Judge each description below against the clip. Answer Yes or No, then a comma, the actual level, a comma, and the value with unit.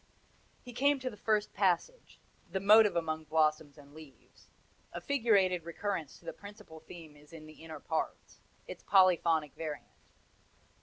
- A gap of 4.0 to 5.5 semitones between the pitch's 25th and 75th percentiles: Yes, average, 4.8 semitones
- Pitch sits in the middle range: Yes, medium, 170 Hz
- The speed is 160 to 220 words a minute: No, average, 150 wpm